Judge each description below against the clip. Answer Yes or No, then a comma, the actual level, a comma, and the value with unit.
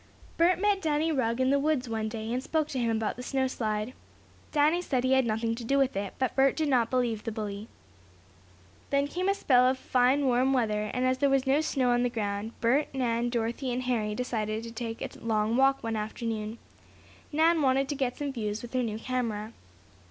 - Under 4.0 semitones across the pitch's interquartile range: Yes, average, 3.2 semitones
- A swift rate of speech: Yes, fast, 220 wpm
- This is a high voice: Yes, very high, 250 Hz